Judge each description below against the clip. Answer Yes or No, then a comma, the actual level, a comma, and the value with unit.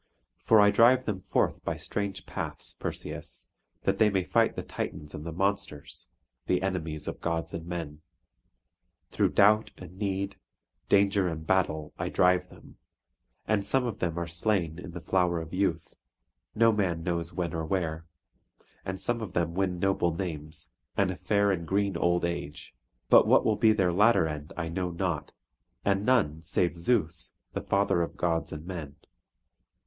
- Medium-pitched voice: No, very low, 90 Hz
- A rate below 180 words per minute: Yes, average, 170 wpm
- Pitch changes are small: No, average, 3.2 semitones